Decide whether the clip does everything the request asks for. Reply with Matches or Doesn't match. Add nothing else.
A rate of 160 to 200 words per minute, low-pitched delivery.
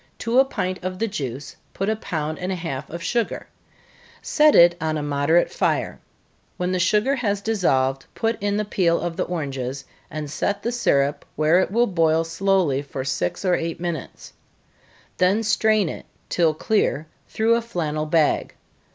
Doesn't match